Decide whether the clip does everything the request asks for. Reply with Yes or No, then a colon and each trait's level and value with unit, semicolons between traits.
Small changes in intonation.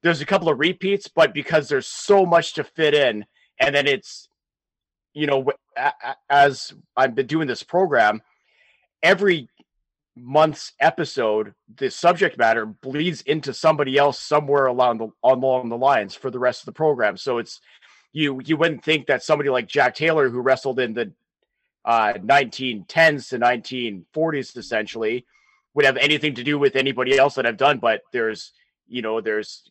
No: average, 3.8 semitones